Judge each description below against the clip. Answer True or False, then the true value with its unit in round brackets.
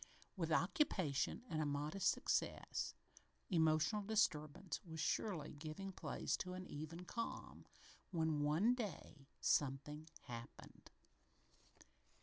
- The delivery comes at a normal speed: False (105 wpm)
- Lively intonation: False (4.2 semitones)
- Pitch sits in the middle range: True (160 Hz)